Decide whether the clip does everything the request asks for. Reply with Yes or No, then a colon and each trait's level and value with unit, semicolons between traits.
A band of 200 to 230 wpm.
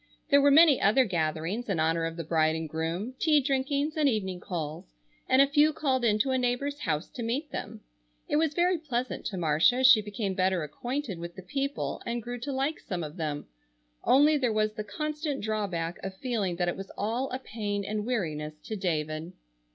Yes: fast, 205 wpm